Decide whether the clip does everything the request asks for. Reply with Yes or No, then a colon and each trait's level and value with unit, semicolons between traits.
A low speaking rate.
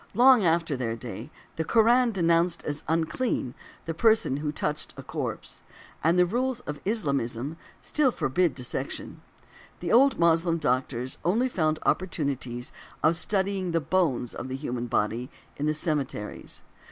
No: average, 150 wpm